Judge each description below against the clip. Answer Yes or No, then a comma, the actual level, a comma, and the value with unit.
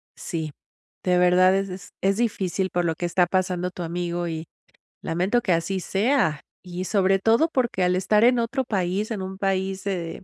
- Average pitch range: No, narrow, 2.0 semitones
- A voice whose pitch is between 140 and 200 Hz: Yes, medium, 185 Hz